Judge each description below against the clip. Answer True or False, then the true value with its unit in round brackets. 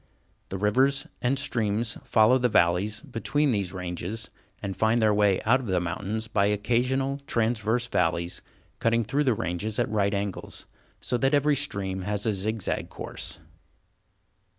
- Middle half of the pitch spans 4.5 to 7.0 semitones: False (3.7 semitones)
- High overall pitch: False (110 Hz)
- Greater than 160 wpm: False (155 wpm)